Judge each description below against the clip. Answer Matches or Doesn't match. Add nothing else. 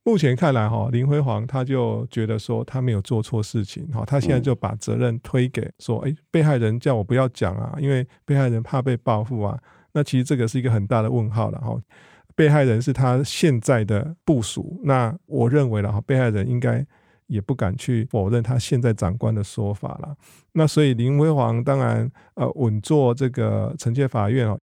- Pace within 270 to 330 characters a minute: Matches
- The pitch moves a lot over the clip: Doesn't match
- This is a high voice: Doesn't match